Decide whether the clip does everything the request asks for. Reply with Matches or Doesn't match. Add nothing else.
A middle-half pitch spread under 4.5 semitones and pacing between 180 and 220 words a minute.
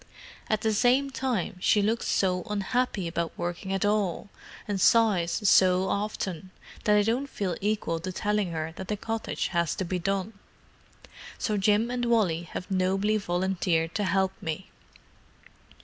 Doesn't match